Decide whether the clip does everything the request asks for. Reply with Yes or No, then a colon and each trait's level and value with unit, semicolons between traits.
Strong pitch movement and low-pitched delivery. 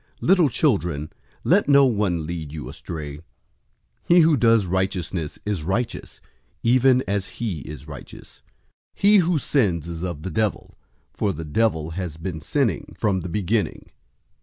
Yes: wide, 6.8 semitones; very low, 95 Hz